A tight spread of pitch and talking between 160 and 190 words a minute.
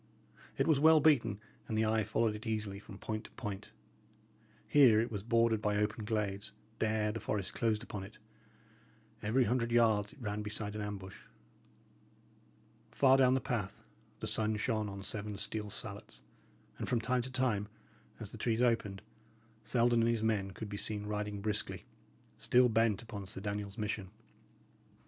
Yes: narrow, 2.1 semitones; average, 165 wpm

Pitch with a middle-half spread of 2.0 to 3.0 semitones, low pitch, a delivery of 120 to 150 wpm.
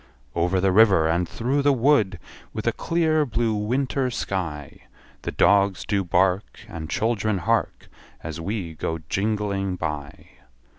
No: average, 4.8 semitones; low, 100 Hz; average, 140 wpm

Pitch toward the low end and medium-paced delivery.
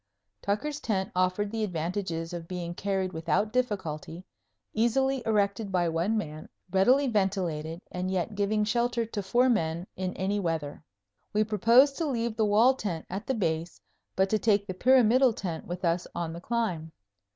No: high, 200 Hz; average, 165 wpm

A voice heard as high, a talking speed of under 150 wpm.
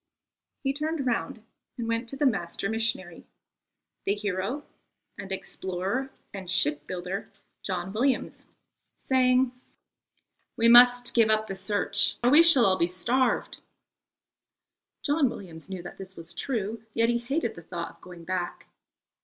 Yes: high, 215 Hz; average, 140 wpm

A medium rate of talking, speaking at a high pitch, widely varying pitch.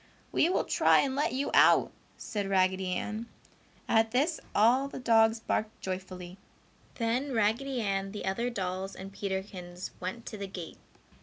No: average, 155 wpm; high, 210 Hz; average, 3.8 semitones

